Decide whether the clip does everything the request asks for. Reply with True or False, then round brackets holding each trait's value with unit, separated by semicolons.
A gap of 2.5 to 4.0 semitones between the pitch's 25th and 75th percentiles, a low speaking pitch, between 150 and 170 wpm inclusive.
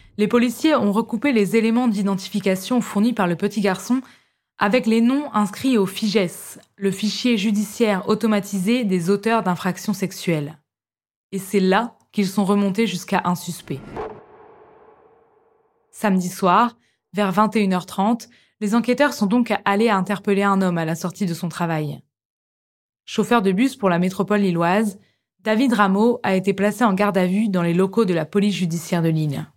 False (3.6 semitones; 205 Hz; 160 wpm)